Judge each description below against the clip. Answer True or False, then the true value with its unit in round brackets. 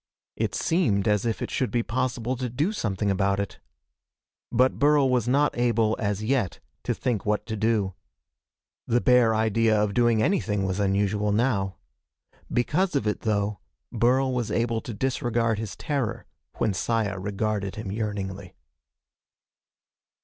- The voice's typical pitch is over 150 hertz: False (110 Hz)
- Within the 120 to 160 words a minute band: True (150 wpm)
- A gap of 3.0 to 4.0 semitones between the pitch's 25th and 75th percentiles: True (3.3 semitones)